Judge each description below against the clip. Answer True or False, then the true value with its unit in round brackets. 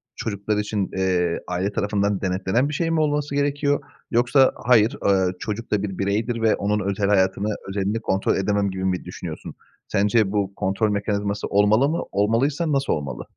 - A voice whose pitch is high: False (105 Hz)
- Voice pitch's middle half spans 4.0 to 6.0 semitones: False (3.3 semitones)